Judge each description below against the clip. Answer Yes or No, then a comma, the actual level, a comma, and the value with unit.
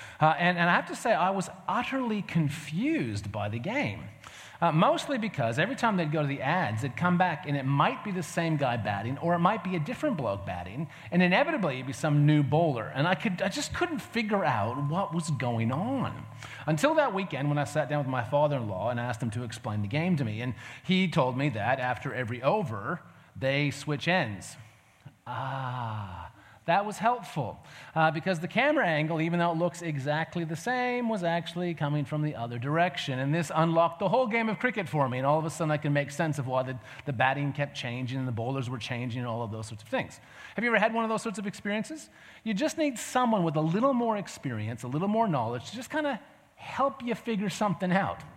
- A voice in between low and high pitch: Yes, medium, 155 Hz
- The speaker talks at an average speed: No, fast, 230 wpm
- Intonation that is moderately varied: No, wide, 6.8 semitones